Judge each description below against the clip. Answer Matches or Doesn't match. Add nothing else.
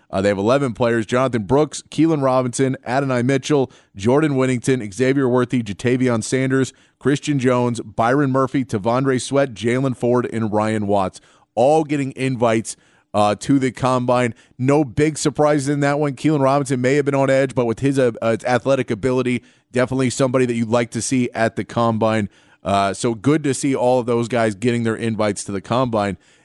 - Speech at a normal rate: Matches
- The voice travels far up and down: Doesn't match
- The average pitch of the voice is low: Matches